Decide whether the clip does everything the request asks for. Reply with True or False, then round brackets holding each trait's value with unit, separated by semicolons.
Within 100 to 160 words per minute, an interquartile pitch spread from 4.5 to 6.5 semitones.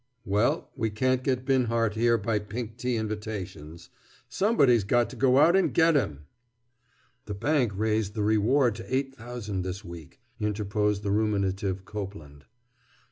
False (145 wpm; 3.6 semitones)